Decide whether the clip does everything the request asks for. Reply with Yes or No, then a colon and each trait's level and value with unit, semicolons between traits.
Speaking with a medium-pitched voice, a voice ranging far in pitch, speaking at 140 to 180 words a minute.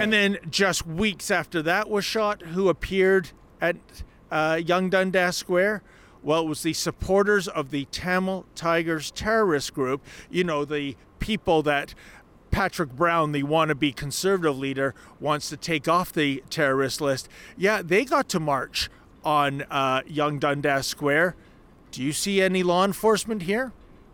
No: medium, 165 Hz; average, 4.8 semitones; average, 150 wpm